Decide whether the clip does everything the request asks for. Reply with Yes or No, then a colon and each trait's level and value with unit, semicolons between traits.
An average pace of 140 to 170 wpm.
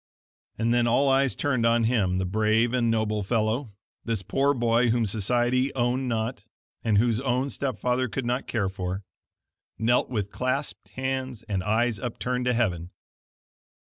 Yes: average, 160 wpm